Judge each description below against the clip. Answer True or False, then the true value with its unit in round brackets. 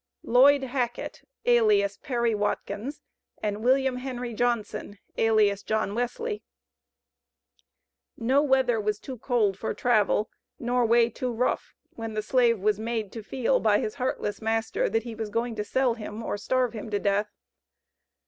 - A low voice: False (230 Hz)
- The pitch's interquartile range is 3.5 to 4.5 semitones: False (2.7 semitones)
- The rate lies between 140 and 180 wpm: True (150 wpm)